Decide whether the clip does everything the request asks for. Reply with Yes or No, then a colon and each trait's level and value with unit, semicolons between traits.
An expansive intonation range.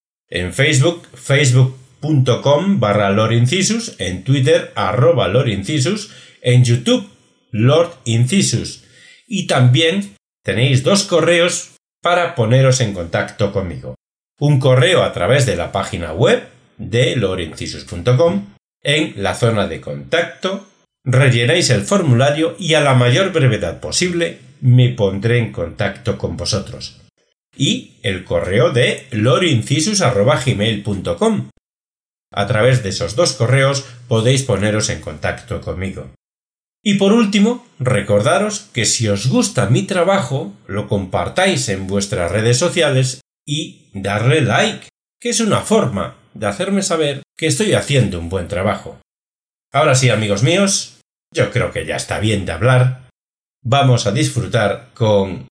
Yes: wide, 7.4 semitones